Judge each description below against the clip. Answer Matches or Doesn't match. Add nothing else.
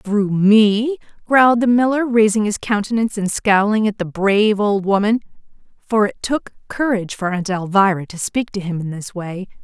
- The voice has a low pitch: Doesn't match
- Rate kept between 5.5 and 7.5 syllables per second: Doesn't match